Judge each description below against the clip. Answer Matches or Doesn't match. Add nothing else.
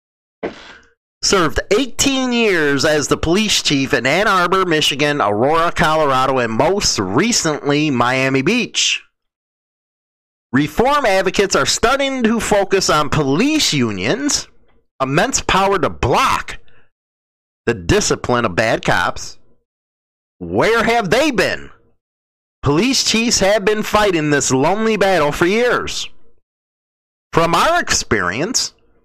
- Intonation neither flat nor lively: Doesn't match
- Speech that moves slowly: Matches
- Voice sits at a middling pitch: Matches